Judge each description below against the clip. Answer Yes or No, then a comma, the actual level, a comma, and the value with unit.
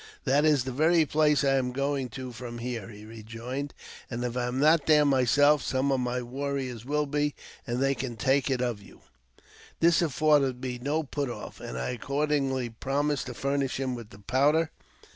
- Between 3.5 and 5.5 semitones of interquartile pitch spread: No, average, 2.9 semitones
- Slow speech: No, average, 195 wpm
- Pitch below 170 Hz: Yes, low, 135 Hz